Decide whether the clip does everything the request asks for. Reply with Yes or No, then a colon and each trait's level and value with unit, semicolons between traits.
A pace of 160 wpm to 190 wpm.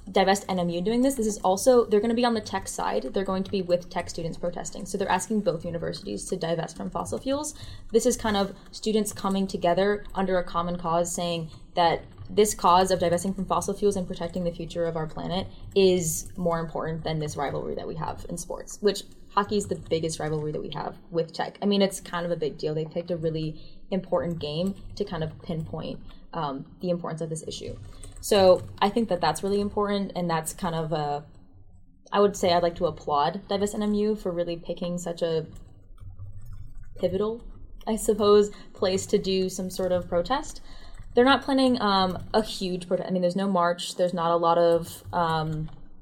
No: fast, 205 wpm